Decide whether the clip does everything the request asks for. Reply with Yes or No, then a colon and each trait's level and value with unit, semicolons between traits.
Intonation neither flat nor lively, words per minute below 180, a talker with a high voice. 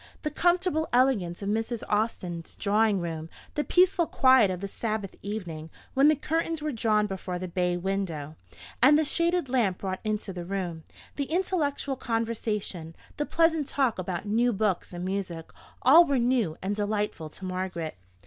No: wide, 6.7 semitones; average, 165 wpm; high, 210 Hz